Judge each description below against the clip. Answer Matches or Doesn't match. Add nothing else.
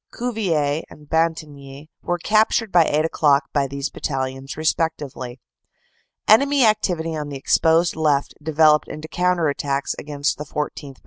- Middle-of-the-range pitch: Matches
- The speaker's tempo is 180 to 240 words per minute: Doesn't match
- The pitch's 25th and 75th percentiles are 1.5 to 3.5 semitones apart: Matches